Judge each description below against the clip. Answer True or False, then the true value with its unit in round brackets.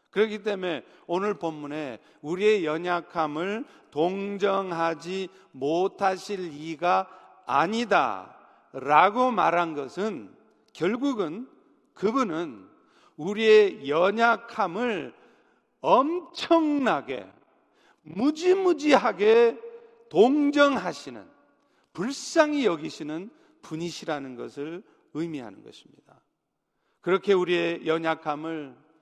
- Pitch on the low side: False (190 Hz)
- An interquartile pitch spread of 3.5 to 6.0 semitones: False (6.4 semitones)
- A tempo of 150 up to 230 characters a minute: True (200 characters per minute)